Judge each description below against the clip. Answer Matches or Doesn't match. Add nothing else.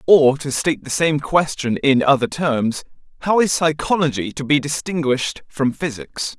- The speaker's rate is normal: Matches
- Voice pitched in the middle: Matches